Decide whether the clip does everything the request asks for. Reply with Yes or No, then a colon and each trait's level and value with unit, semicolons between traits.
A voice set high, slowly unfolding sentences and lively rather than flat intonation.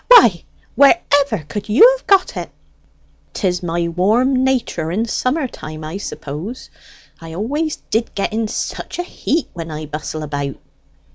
No: high, 210 Hz; average, 150 wpm; wide, 8.6 semitones